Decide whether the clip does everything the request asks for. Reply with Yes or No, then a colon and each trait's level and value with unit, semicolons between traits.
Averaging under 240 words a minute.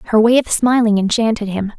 Yes: average, 200 wpm